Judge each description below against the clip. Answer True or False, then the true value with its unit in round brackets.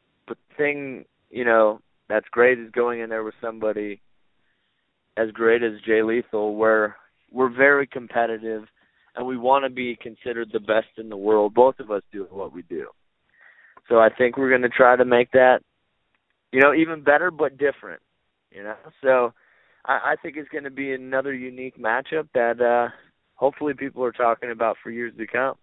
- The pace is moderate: True (185 wpm)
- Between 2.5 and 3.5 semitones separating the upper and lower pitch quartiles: True (2.9 semitones)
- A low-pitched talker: True (120 Hz)